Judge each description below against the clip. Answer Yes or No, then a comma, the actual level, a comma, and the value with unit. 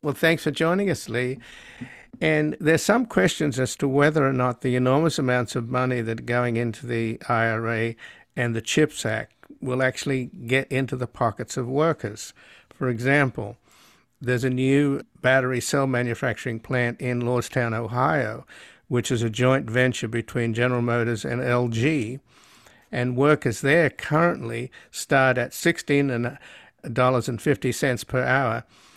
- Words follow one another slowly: No, average, 145 wpm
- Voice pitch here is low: Yes, low, 125 Hz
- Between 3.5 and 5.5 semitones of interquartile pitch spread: No, narrow, 2.5 semitones